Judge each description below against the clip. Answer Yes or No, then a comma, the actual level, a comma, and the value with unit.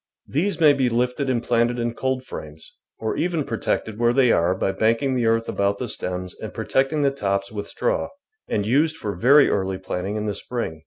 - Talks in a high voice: No, low, 115 Hz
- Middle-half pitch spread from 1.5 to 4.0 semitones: No, average, 4.8 semitones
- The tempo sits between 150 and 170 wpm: No, average, 200 wpm